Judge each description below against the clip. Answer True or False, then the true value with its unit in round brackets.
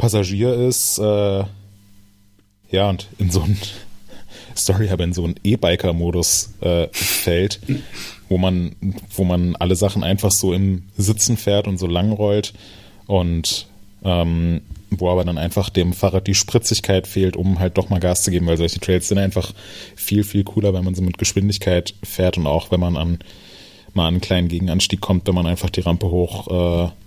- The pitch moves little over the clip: True (2.1 semitones)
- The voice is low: True (95 Hz)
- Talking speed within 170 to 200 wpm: True (180 wpm)